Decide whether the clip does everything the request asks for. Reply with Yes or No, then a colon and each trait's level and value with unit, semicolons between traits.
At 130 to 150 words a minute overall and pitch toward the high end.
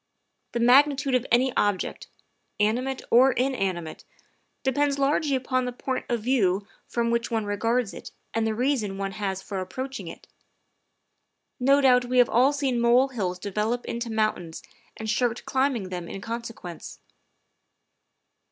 Yes: average, 145 wpm; high, 235 Hz